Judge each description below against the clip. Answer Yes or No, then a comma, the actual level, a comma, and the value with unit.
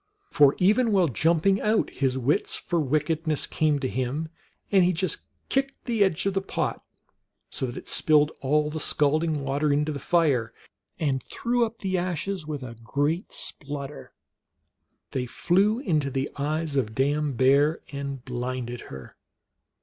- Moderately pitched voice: Yes, medium, 150 Hz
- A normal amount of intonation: Yes, average, 4.4 semitones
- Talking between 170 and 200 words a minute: No, average, 160 wpm